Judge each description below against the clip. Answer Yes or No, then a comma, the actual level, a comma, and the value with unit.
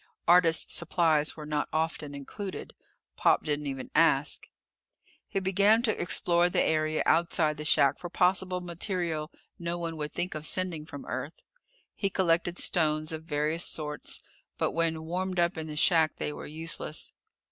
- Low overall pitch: No, medium, 165 Hz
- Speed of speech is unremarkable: Yes, average, 160 wpm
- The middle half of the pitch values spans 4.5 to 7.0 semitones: No, narrow, 2.6 semitones